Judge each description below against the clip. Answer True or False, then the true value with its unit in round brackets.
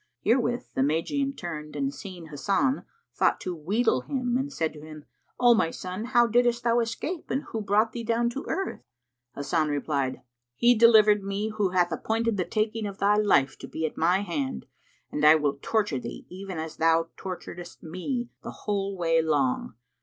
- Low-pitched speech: False (195 Hz)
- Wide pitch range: True (6.5 semitones)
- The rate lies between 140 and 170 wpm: False (185 wpm)